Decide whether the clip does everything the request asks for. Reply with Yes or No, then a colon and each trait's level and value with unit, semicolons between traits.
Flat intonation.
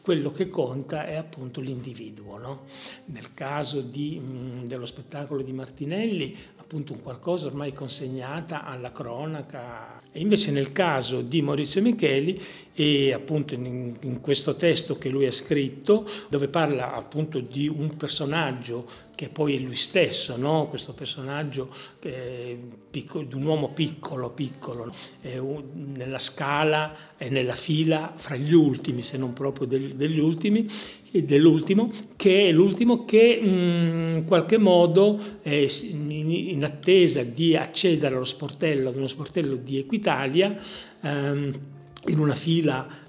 No: average, 3.6 semitones